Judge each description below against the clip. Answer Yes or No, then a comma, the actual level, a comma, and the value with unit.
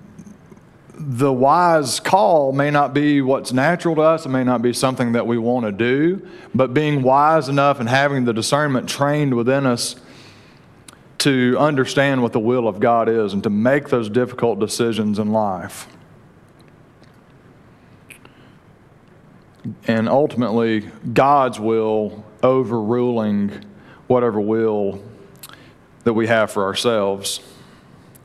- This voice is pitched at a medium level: No, low, 125 Hz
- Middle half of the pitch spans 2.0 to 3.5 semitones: No, average, 4.0 semitones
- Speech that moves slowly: Yes, slow, 125 wpm